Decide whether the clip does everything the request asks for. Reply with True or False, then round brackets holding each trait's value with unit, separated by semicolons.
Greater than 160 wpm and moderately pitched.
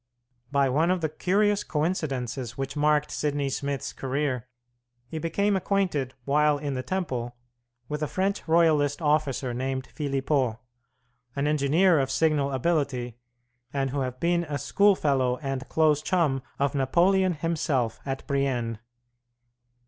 False (135 wpm; 145 Hz)